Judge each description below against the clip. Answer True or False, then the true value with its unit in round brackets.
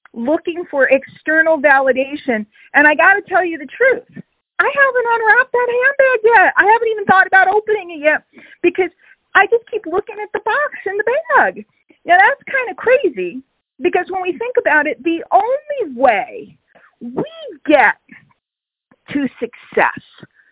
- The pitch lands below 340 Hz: False (365 Hz)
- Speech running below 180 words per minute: True (160 wpm)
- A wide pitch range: True (6.2 semitones)